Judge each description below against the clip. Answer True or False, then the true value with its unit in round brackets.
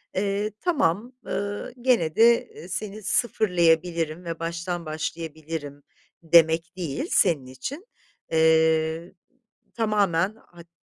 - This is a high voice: False (170 Hz)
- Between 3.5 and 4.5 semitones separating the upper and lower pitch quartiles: True (4.2 semitones)